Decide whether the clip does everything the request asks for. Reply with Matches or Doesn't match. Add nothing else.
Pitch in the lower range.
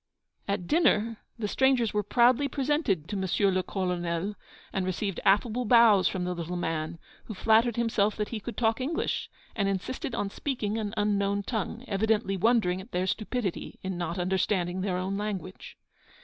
Doesn't match